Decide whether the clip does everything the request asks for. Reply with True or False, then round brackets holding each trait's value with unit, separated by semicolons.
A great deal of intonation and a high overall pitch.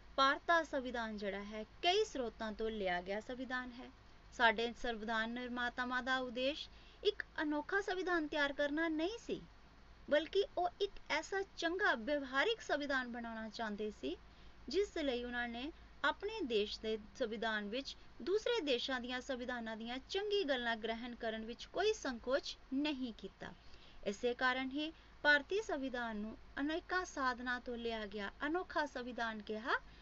True (5.8 semitones; 260 Hz)